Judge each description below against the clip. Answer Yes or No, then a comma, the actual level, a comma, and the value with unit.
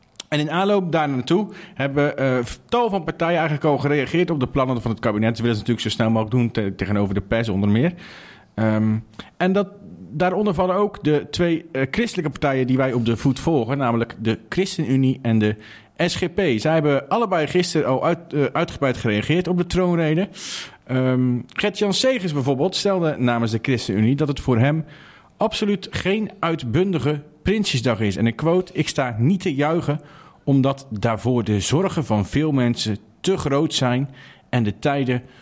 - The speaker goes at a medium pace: Yes, average, 175 wpm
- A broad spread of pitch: Yes, wide, 6.5 semitones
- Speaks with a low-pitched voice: No, medium, 145 Hz